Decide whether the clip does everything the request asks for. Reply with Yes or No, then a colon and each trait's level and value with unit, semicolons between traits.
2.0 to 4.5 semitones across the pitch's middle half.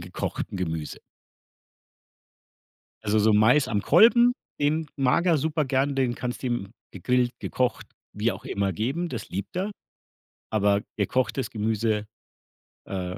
No: wide, 5.4 semitones